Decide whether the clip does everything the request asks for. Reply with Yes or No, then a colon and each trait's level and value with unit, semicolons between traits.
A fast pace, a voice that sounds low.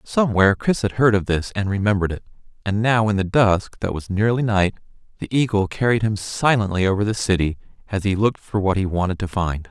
Yes: fast, 215 wpm; low, 105 Hz